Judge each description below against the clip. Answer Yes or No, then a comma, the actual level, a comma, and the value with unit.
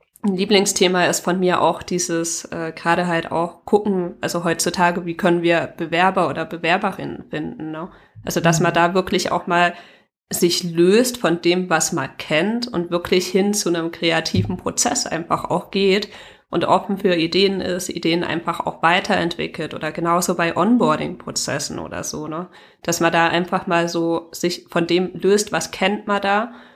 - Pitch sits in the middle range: Yes, medium, 175 Hz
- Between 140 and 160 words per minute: No, average, 170 wpm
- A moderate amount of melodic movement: No, narrow, 2.1 semitones